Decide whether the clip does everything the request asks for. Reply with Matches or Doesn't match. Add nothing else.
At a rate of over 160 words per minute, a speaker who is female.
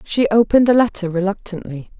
Doesn't match